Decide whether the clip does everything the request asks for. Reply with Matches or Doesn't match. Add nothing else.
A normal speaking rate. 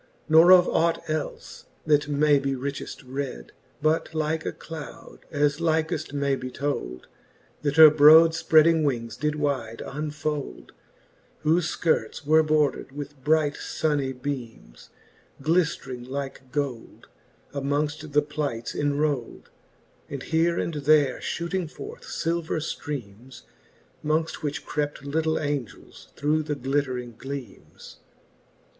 Doesn't match